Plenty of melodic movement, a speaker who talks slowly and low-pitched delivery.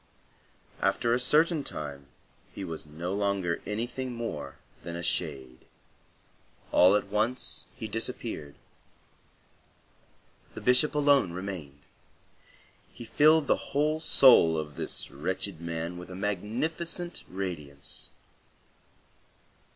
Yes: wide, 7.4 semitones; slow, 105 wpm; low, 100 Hz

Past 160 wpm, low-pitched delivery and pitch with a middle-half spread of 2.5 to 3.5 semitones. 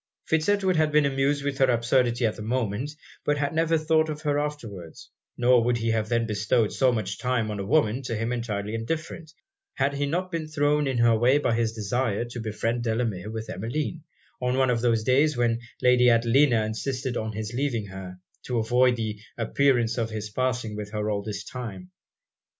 No: average, 200 wpm; low, 120 Hz; average, 4.1 semitones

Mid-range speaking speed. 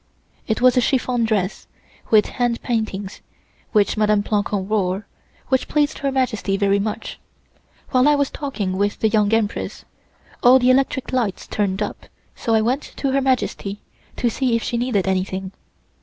Yes: average, 170 wpm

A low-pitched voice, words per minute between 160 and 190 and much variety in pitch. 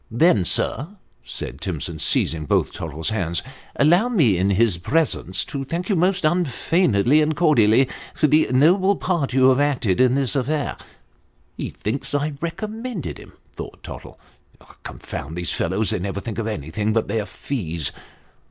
Yes: low, 130 Hz; average, 170 wpm; wide, 8.3 semitones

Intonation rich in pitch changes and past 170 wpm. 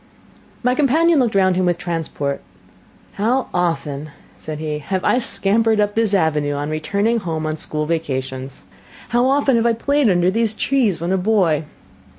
No: wide, 6.6 semitones; average, 165 wpm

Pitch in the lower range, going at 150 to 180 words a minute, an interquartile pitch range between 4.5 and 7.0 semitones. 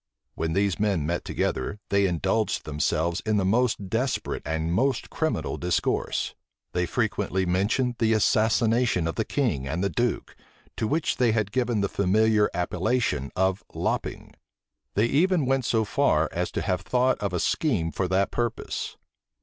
Yes: low, 100 Hz; average, 160 wpm; average, 5.0 semitones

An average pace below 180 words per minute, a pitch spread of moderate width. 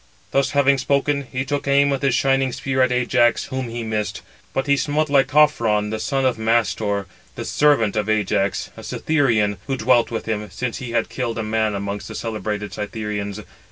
No: average, 190 wpm; average, 4.3 semitones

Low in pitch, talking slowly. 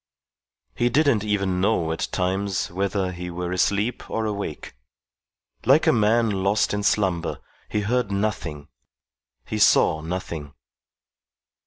Yes: low, 100 Hz; slow, 125 wpm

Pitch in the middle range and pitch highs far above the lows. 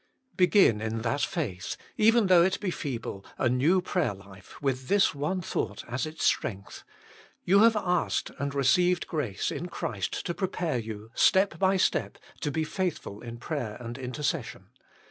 Yes: medium, 145 Hz; wide, 8.0 semitones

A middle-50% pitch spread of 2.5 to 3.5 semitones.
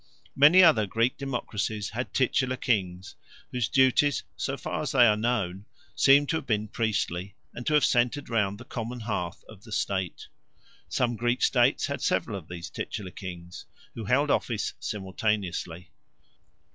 No: average, 4.5 semitones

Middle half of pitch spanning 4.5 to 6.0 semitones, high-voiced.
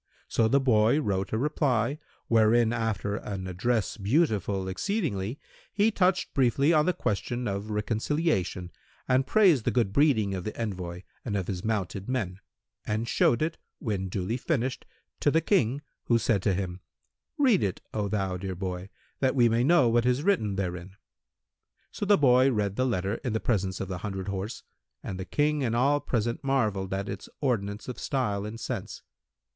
No: average, 5.3 semitones; low, 110 Hz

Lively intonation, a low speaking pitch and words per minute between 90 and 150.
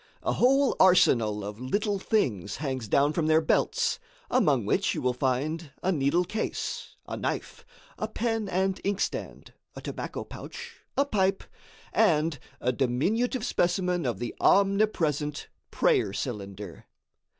No: wide, 8.0 semitones; medium, 165 Hz; slow, 135 wpm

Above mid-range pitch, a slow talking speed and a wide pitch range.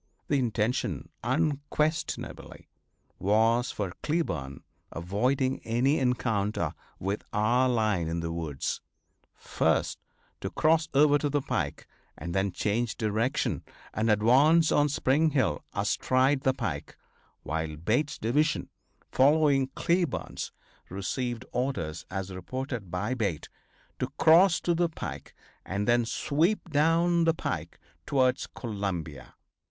No: low, 125 Hz; slow, 115 wpm; wide, 6.7 semitones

